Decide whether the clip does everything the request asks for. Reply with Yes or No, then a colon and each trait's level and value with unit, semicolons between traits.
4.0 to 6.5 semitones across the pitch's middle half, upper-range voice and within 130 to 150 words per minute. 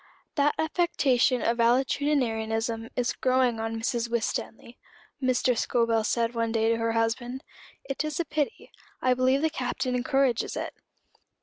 No: average, 2.7 semitones; high, 245 Hz; average, 140 wpm